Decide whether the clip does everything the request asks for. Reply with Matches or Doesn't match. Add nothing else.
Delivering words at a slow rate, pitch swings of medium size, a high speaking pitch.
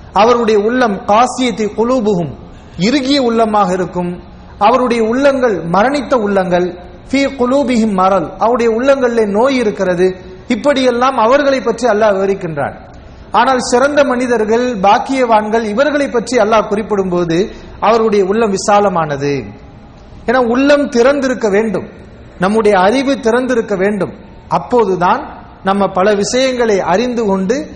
Matches